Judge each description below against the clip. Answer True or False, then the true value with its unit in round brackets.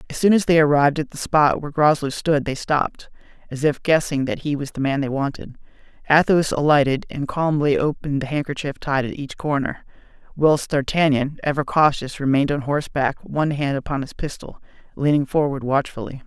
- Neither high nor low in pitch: True (145 Hz)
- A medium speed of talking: True (180 wpm)